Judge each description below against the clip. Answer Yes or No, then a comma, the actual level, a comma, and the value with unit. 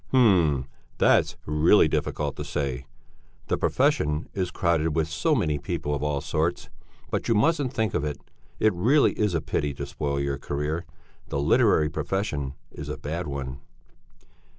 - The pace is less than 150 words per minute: No, average, 160 wpm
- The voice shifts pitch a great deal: No, average, 4.0 semitones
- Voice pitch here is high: No, very low, 75 Hz